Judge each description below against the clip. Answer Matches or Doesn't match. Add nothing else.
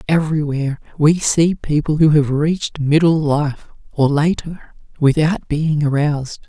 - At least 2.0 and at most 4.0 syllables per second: Doesn't match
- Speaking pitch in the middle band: Matches